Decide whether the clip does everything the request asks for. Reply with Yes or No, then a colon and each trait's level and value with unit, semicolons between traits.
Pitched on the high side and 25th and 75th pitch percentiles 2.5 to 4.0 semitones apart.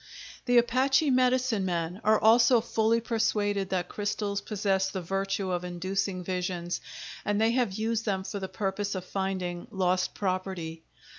Yes: high, 195 Hz; average, 3.2 semitones